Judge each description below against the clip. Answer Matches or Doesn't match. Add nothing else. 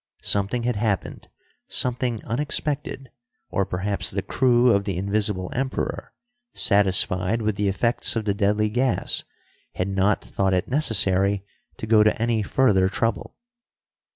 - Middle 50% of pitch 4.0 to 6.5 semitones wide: Doesn't match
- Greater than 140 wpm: Doesn't match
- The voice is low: Matches